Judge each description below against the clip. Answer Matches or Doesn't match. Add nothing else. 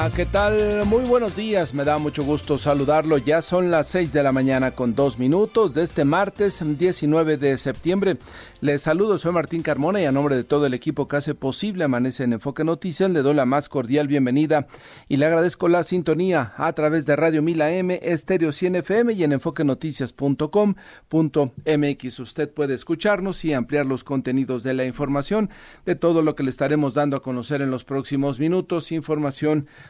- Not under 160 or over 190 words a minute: Matches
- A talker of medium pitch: Matches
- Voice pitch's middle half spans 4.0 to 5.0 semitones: Doesn't match